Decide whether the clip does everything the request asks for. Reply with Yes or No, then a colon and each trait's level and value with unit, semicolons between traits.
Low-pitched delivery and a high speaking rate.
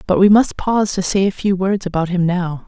No: medium, 185 Hz; fast, 270 wpm